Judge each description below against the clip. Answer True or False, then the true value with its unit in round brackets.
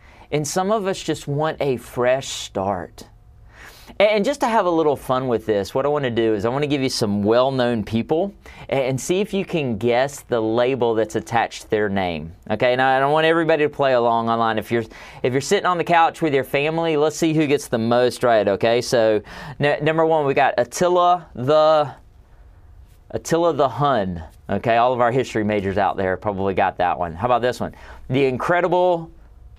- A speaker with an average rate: False (210 wpm)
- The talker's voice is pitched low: True (130 Hz)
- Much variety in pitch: True (5.8 semitones)